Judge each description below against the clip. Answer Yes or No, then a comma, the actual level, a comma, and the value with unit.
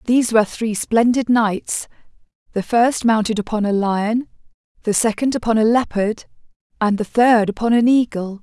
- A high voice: Yes, high, 225 Hz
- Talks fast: No, average, 155 wpm